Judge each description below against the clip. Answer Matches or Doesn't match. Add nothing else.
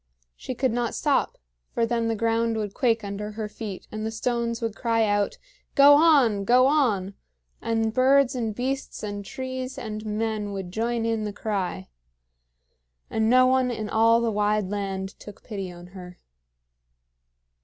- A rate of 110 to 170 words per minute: Matches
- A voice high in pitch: Matches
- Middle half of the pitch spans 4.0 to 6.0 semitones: Doesn't match